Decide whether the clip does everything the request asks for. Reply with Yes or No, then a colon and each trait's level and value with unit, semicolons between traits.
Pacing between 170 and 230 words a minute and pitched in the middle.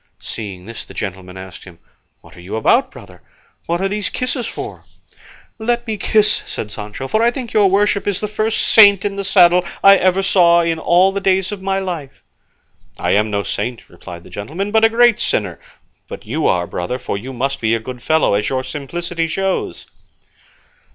Yes: average, 195 wpm; medium, 170 Hz